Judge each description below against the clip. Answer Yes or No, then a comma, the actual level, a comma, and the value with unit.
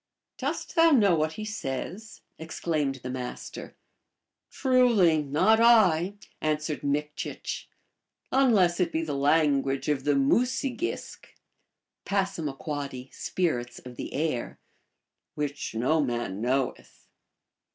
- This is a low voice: No, medium, 155 Hz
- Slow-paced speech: Yes, slow, 130 wpm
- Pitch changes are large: Yes, wide, 6.4 semitones